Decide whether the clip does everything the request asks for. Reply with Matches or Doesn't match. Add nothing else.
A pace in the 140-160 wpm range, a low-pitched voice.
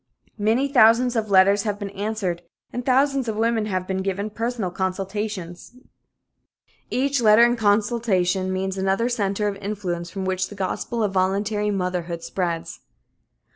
Doesn't match